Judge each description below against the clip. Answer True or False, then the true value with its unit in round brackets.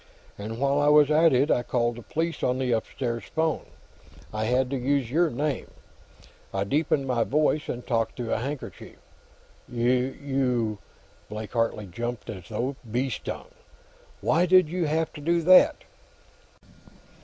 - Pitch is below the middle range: True (130 Hz)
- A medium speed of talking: True (155 wpm)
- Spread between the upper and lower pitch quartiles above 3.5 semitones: True (4.2 semitones)